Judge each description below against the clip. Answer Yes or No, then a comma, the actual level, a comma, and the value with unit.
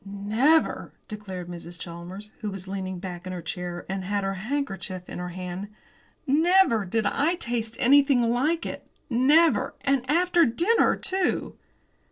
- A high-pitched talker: Yes, high, 210 Hz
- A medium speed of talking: Yes, average, 150 wpm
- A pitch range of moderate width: No, wide, 7.3 semitones